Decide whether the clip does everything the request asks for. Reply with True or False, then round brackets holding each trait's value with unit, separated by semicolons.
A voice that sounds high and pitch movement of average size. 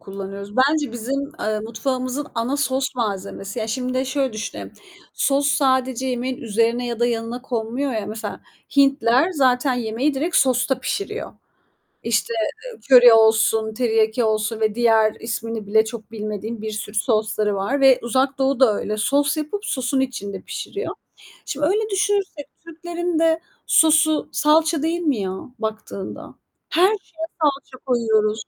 True (250 Hz; 4.3 semitones)